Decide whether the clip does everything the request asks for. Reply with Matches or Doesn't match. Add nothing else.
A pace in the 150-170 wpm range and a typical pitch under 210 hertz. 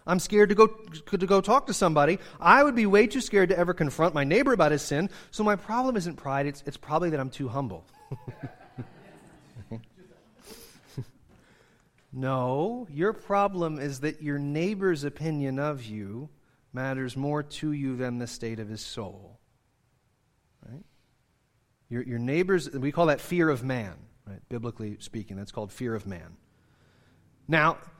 Matches